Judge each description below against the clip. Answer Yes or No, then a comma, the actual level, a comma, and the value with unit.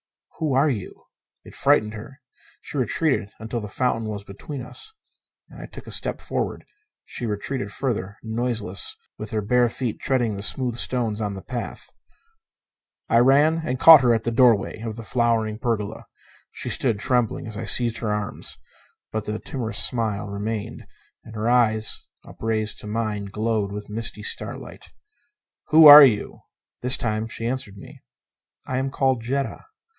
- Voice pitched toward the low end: Yes, low, 115 Hz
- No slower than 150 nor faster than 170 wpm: Yes, average, 165 wpm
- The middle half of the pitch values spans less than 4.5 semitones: Yes, average, 3.0 semitones